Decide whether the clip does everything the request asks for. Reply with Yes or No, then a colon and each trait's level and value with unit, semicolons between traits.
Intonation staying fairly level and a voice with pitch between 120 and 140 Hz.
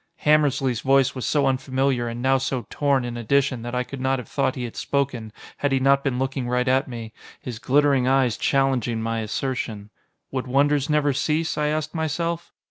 Yes: narrow, 2.3 semitones; low, 135 Hz